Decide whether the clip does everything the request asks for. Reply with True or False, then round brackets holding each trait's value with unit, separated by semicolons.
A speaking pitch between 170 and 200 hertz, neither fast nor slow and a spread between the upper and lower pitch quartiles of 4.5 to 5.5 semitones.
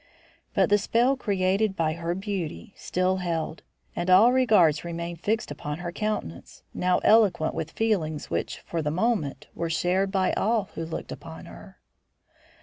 False (185 Hz; 155 wpm; 4.1 semitones)